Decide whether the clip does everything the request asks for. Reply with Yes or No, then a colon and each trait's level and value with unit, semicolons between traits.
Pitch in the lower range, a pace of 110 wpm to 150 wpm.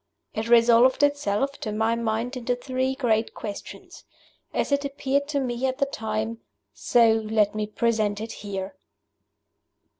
No: high, 230 Hz; average, 145 wpm